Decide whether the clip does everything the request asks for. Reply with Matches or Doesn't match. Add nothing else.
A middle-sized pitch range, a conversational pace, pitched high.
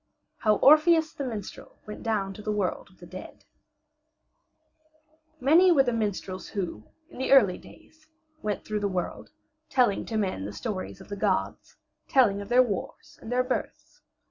Matches